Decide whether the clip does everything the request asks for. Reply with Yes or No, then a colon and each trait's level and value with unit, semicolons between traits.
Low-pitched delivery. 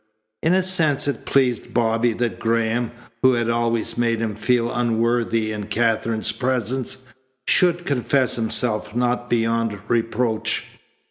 Yes: low, 115 Hz